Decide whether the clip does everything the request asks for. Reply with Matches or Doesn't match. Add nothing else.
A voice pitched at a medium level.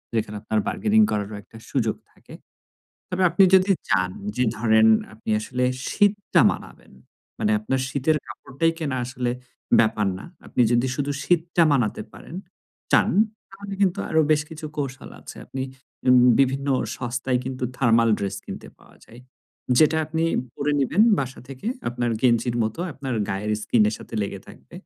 Doesn't match